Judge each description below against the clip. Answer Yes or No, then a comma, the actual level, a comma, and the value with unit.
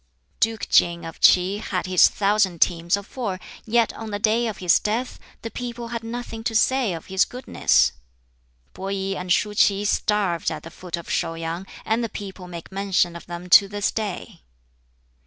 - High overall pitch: Yes, high, 200 Hz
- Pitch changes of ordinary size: Yes, average, 3.9 semitones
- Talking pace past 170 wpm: Yes, average, 190 wpm